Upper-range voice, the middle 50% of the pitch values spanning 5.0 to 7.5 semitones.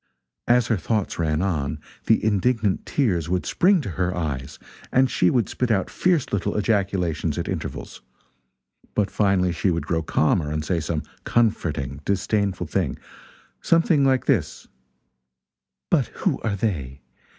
No: very low, 95 Hz; wide, 5.6 semitones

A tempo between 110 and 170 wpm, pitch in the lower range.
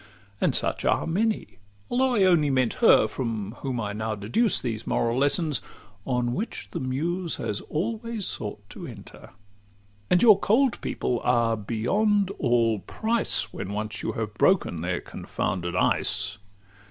Yes: average, 150 wpm; low, 125 Hz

